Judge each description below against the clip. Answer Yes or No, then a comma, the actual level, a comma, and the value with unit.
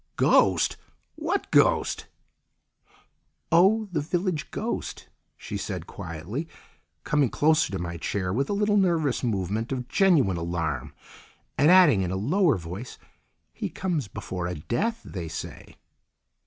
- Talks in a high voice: No, low, 135 Hz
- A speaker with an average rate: No, slow, 130 wpm